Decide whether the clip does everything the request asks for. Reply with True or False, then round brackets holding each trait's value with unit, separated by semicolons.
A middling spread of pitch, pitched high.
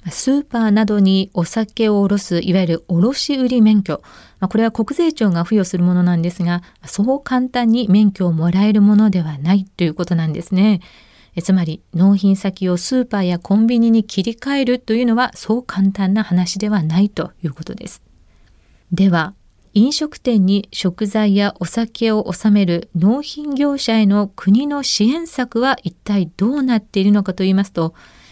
True (4.1 semitones; 200 Hz)